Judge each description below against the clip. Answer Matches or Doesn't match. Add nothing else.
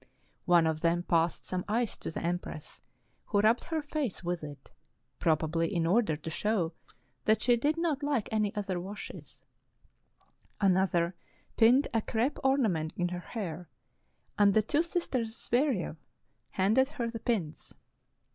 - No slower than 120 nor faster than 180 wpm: Matches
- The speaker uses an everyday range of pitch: Doesn't match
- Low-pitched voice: Doesn't match